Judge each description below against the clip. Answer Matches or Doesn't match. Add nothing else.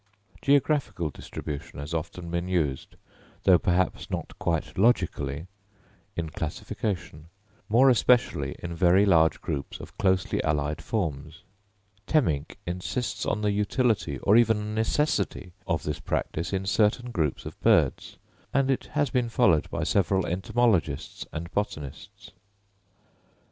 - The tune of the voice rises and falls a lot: Matches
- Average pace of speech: Doesn't match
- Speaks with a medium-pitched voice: Doesn't match